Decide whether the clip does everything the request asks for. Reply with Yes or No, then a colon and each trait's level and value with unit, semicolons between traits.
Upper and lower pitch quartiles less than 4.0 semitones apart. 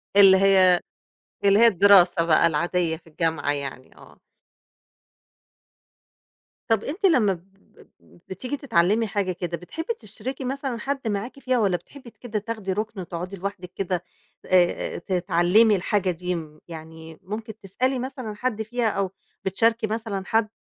No: average, 4.5 semitones